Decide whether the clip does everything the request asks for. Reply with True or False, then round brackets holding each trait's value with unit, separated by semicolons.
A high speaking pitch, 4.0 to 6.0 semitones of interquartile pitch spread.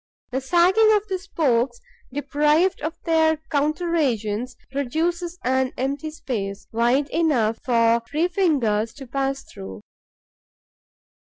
True (280 Hz; 5.5 semitones)